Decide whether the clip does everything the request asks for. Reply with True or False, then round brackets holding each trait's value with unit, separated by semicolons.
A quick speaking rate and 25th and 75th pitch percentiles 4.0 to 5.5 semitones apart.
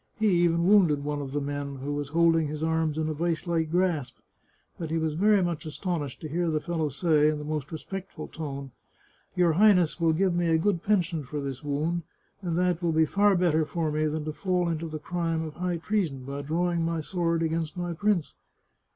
False (220 wpm; 2.5 semitones)